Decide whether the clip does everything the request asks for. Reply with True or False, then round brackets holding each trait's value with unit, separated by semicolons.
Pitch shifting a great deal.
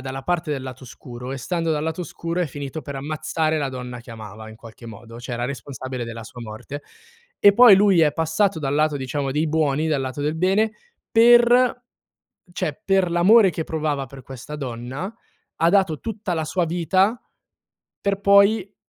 True (5.8 semitones)